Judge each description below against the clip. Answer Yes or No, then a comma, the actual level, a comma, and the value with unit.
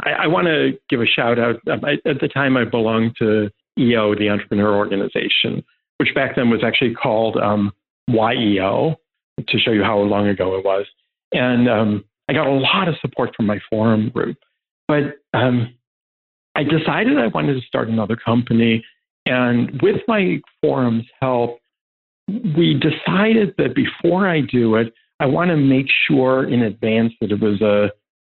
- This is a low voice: Yes, low, 115 Hz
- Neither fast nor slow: Yes, average, 170 wpm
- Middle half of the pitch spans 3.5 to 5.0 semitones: Yes, average, 4.5 semitones